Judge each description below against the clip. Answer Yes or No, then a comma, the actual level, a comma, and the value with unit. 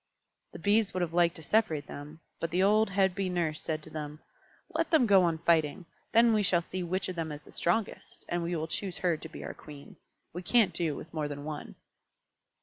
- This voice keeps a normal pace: No, fast, 230 wpm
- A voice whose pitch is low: No, medium, 170 Hz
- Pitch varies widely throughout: No, average, 3.6 semitones